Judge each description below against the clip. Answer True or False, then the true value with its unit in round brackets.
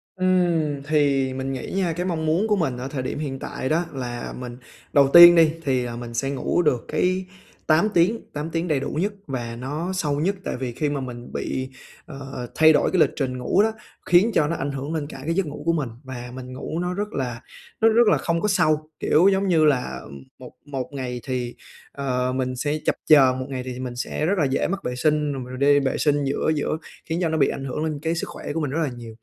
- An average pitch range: True (4.3 semitones)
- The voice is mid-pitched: True (145 Hz)